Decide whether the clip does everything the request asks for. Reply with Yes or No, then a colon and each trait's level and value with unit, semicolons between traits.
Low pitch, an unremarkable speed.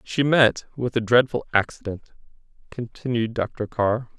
No: low, 120 Hz; slow, 130 wpm